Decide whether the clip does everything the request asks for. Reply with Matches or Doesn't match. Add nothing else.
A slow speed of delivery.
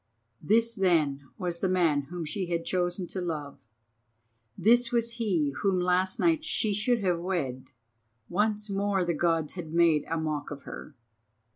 Doesn't match